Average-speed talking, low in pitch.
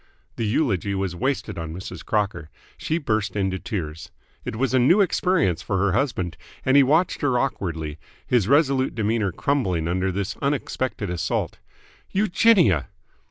Yes: average, 150 wpm; low, 105 Hz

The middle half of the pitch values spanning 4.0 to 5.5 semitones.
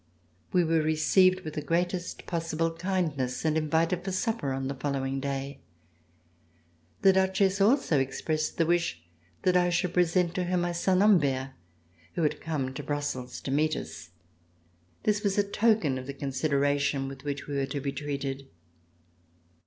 Yes: average, 4.5 semitones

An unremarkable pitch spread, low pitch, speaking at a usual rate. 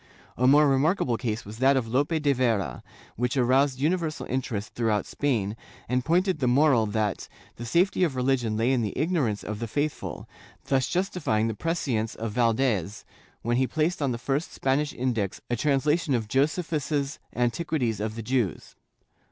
Yes: average, 4.5 semitones; low, 130 Hz; average, 170 wpm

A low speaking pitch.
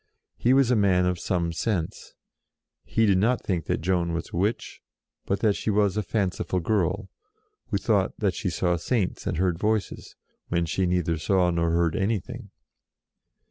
Yes: very low, 95 Hz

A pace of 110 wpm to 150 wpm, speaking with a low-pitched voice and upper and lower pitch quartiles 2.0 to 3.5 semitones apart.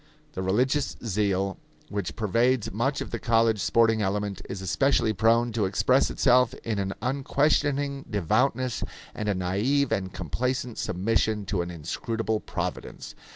No: average, 140 wpm; low, 110 Hz; average, 4.4 semitones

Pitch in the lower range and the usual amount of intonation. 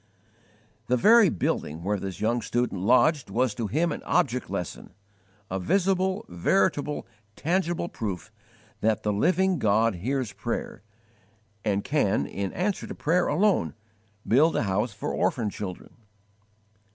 No: low, 120 Hz; wide, 9.0 semitones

